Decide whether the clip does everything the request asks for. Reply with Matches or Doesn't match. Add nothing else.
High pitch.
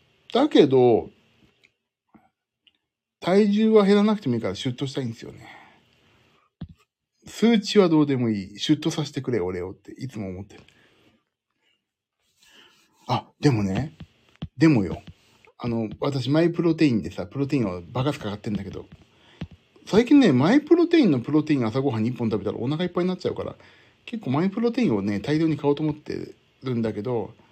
Doesn't match